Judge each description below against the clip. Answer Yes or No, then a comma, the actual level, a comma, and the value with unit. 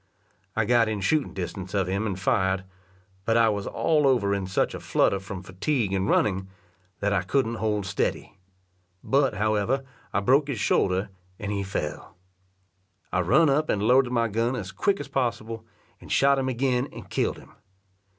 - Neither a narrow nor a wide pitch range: Yes, average, 4.8 semitones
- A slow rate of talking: No, average, 180 wpm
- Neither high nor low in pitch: No, low, 110 Hz